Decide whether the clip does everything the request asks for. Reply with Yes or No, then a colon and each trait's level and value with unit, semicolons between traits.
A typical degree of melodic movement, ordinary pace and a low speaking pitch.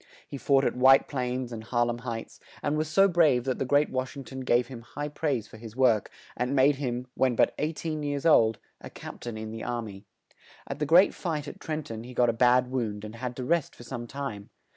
No: average, 3.3 semitones; fast, 250 wpm; low, 130 Hz